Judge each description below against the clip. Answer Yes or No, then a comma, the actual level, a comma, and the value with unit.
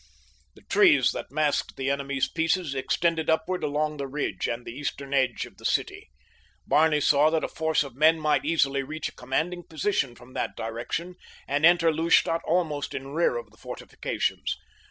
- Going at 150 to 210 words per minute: Yes, average, 175 wpm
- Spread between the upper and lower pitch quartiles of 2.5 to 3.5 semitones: Yes, average, 3.0 semitones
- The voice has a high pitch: No, medium, 150 Hz